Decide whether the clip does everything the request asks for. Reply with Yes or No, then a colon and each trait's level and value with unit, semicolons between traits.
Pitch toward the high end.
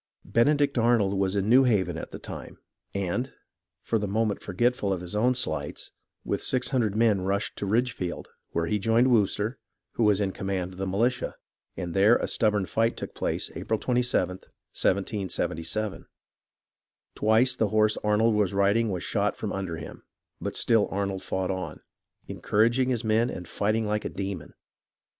No: low, 105 Hz